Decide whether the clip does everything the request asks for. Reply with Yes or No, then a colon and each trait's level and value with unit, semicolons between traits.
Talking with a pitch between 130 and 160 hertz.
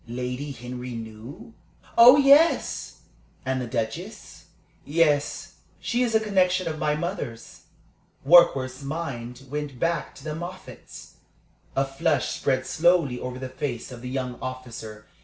Yes: low, 135 Hz